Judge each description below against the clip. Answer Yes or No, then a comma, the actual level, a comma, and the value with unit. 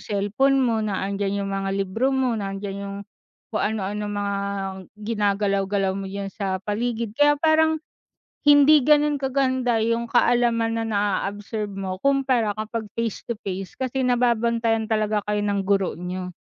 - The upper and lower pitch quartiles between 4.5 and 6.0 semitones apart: No, average, 3.5 semitones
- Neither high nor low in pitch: No, high, 215 Hz